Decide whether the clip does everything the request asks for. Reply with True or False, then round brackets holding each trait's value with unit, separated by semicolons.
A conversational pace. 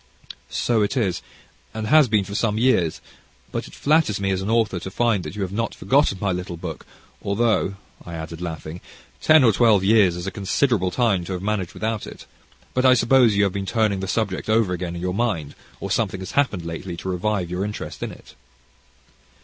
False (210 wpm)